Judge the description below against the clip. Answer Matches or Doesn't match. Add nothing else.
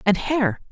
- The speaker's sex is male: Doesn't match